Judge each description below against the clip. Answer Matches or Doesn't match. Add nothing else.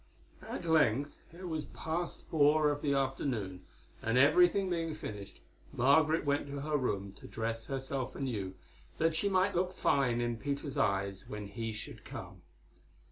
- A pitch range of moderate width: Doesn't match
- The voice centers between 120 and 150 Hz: Matches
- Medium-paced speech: Matches